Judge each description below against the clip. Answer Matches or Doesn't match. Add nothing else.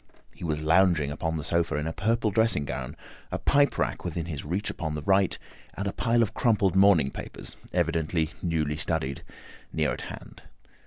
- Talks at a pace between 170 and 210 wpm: Matches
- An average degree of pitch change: Matches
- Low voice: Matches